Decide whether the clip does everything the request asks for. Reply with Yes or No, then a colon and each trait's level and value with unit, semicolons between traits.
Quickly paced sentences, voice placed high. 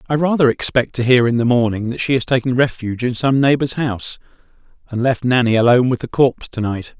No: fast, 225 wpm; low, 125 Hz